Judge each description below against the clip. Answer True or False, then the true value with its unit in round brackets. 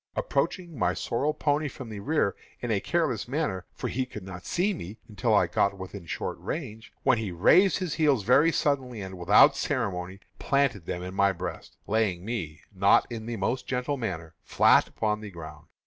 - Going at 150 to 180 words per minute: False (190 wpm)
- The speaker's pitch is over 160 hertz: False (110 Hz)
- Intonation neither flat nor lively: False (6.6 semitones)